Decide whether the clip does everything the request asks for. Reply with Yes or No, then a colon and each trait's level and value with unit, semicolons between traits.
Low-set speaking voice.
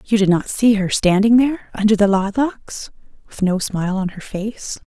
No: high, 205 Hz